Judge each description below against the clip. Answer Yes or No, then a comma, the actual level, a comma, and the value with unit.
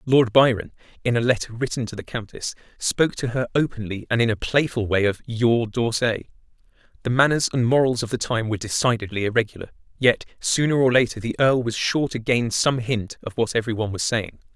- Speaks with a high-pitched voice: No, low, 120 Hz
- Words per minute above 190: Yes, average, 200 wpm